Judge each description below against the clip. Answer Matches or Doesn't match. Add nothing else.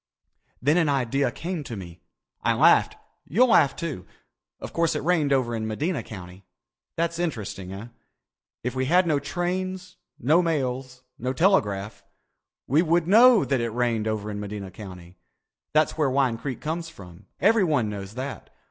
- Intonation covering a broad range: Matches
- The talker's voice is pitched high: Doesn't match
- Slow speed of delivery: Doesn't match